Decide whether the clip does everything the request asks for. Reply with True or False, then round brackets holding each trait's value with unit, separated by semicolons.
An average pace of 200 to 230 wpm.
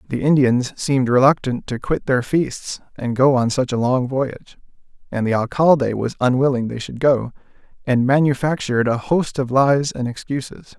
False (175 wpm)